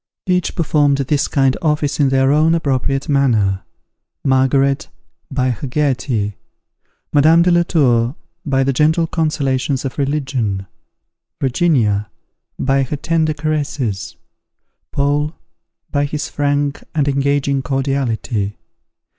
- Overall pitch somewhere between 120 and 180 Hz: Yes, medium, 140 Hz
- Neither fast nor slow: No, slow, 115 wpm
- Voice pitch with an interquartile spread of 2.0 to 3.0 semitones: Yes, narrow, 2.4 semitones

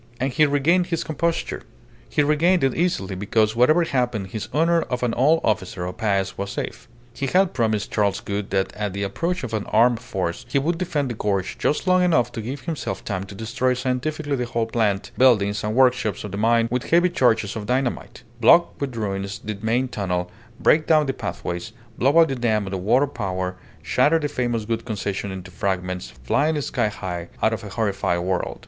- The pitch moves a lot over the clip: Yes, wide, 5.9 semitones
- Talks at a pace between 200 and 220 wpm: Yes, fast, 205 wpm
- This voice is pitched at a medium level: No, low, 115 Hz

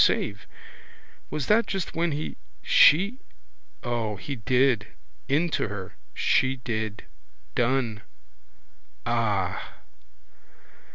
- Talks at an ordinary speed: No, slow, 90 wpm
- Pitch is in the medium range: No, low, 120 Hz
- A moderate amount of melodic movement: No, wide, 5.7 semitones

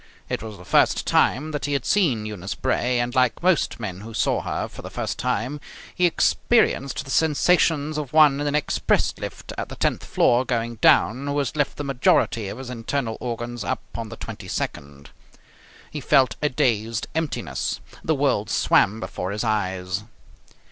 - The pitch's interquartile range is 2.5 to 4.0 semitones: No, average, 4.9 semitones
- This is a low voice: Yes, low, 125 Hz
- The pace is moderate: Yes, average, 180 wpm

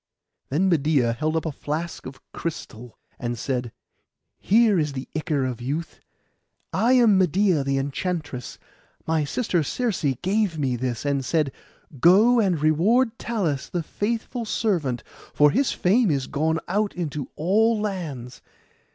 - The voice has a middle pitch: Yes, medium, 160 Hz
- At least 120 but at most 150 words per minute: Yes, average, 145 wpm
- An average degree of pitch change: No, wide, 6.6 semitones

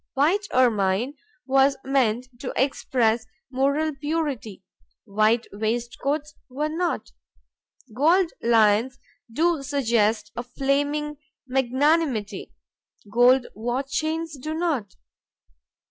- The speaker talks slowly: Yes, slow, 90 wpm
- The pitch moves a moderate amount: Yes, average, 4.5 semitones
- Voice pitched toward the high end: Yes, very high, 265 Hz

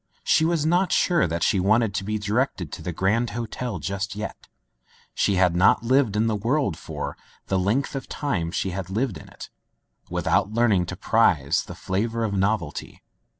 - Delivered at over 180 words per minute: Yes, average, 190 wpm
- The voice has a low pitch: Yes, low, 105 Hz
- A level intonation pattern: No, average, 4.0 semitones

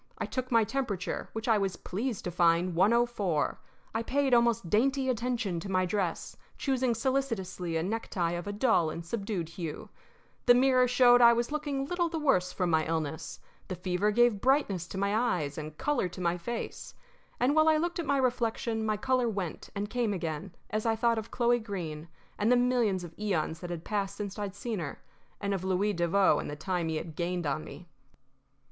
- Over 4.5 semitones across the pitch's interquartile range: Yes, wide, 5.5 semitones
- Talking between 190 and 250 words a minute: Yes, fast, 205 wpm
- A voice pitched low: No, high, 205 Hz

